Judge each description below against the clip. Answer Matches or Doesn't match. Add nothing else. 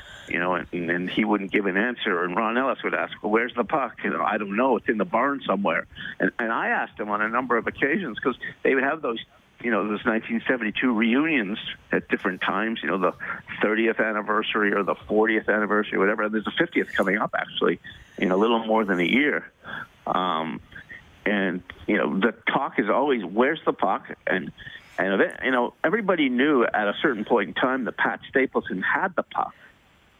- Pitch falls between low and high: Doesn't match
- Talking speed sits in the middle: Doesn't match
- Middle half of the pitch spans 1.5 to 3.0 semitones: Matches